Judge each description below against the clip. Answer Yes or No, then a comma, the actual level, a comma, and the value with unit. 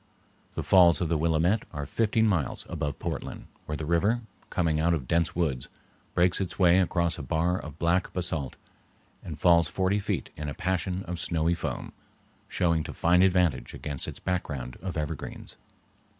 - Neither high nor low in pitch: No, very low, 85 Hz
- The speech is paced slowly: No, average, 170 wpm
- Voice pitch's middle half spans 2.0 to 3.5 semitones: Yes, narrow, 2.6 semitones